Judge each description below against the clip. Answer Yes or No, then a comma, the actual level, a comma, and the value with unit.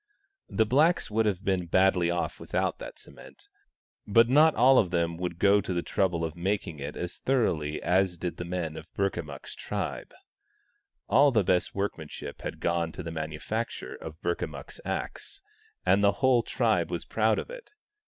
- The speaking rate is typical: Yes, average, 175 wpm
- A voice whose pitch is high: No, very low, 90 Hz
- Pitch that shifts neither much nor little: Yes, average, 4.3 semitones